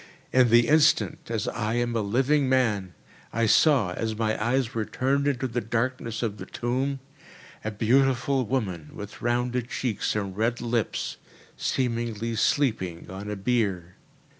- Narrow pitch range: No, average, 3.2 semitones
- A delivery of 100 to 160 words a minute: Yes, average, 150 wpm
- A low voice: Yes, low, 115 Hz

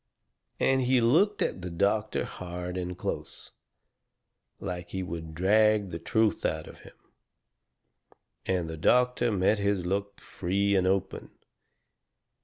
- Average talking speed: No, slow, 130 wpm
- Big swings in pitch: No, average, 3.4 semitones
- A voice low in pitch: Yes, very low, 95 Hz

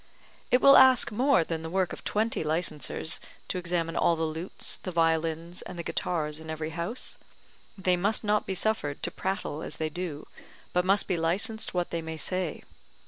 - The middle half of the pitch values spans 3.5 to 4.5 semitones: No, average, 3.1 semitones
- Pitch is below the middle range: No, medium, 175 Hz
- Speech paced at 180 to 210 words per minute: Yes, average, 190 wpm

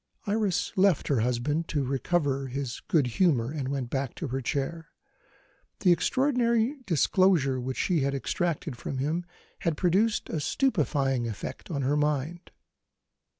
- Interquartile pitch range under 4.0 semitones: No, average, 4.8 semitones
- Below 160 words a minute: Yes, average, 145 wpm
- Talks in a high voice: No, medium, 150 Hz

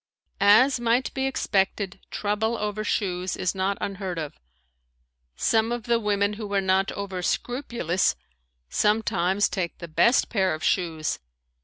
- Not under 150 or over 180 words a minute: No, average, 140 wpm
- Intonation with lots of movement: No, average, 3.1 semitones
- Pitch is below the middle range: No, high, 200 Hz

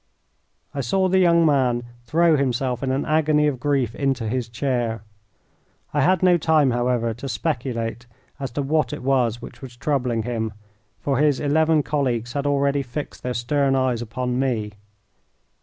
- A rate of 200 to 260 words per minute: No, average, 165 wpm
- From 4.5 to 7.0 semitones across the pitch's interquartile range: No, average, 3.3 semitones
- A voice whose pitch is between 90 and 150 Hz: Yes, low, 135 Hz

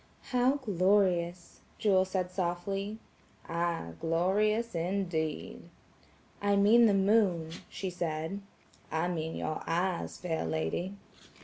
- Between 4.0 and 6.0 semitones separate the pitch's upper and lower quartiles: No, average, 3.2 semitones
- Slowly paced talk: Yes, slow, 105 wpm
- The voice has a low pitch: No, medium, 185 Hz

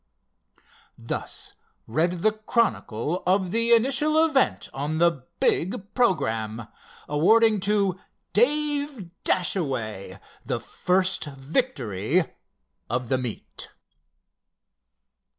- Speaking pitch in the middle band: Yes, medium, 180 Hz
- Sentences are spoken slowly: Yes, slow, 85 wpm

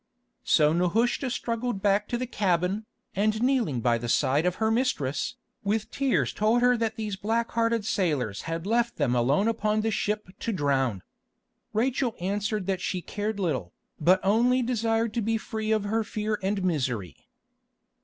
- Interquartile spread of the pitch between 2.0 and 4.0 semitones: No, average, 4.8 semitones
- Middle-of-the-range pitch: No, high, 210 Hz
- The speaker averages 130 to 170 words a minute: Yes, average, 165 wpm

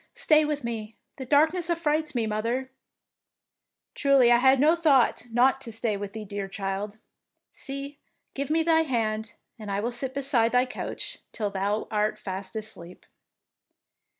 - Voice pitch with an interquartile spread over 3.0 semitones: Yes, average, 4.7 semitones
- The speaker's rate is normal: Yes, average, 160 wpm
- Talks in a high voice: Yes, high, 240 Hz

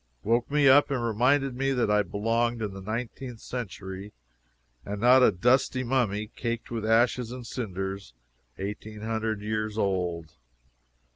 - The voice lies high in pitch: No, low, 115 Hz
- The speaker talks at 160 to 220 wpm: No, average, 150 wpm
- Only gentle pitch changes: No, average, 3.2 semitones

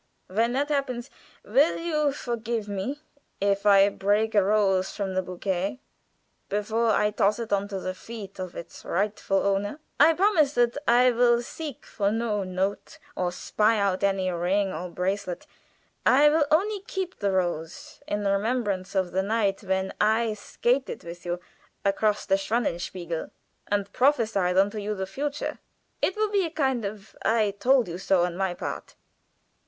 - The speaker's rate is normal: Yes, average, 165 wpm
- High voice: Yes, high, 205 Hz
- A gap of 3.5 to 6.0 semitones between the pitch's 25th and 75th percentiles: Yes, average, 4.1 semitones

